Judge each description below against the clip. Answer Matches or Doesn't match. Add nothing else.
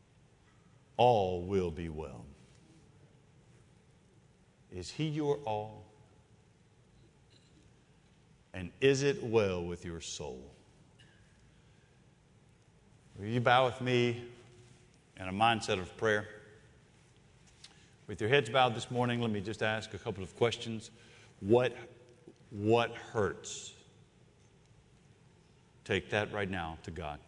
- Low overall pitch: Matches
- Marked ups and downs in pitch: Doesn't match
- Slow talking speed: Matches